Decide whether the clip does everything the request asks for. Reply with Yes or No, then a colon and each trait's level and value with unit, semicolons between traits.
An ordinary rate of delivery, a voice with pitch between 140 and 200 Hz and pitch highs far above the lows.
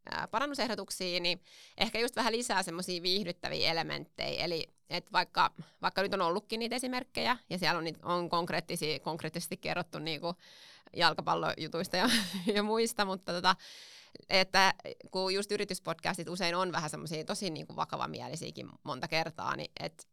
No: average, 140 wpm; medium, 185 Hz; average, 3.3 semitones